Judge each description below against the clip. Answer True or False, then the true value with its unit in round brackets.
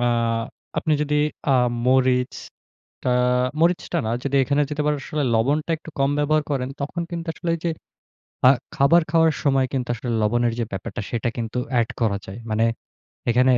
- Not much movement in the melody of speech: False (4.2 semitones)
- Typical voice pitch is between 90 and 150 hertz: True (135 Hz)